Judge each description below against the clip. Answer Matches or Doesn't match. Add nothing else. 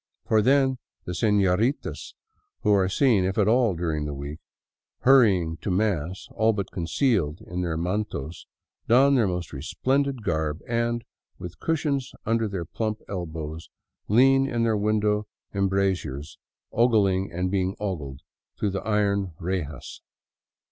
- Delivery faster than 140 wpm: Doesn't match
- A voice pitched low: Matches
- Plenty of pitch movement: Doesn't match